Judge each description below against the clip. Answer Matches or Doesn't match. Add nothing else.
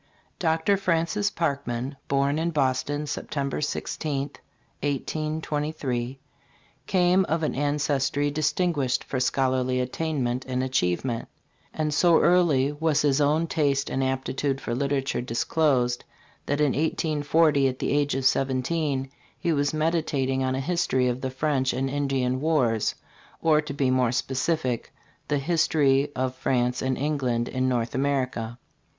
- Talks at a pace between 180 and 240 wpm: Doesn't match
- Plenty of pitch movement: Doesn't match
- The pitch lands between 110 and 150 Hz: Matches